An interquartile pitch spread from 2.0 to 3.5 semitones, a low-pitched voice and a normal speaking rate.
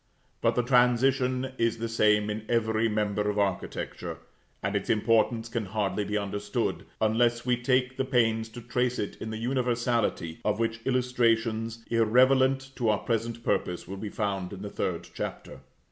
Yes: narrow, 2.6 semitones; low, 115 Hz; average, 165 wpm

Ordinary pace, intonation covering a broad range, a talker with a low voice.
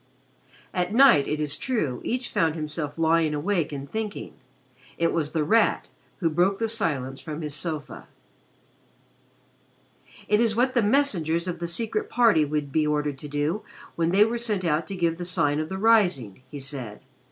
No: average, 175 wpm; wide, 5.9 semitones; medium, 165 Hz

